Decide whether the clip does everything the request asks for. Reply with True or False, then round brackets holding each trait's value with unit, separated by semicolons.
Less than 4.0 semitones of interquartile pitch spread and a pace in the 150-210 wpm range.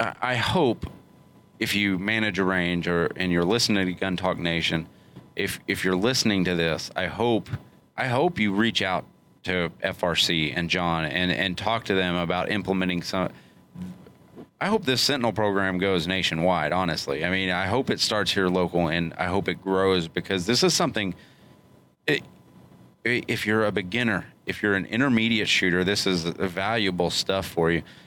True (2.9 semitones; 175 wpm)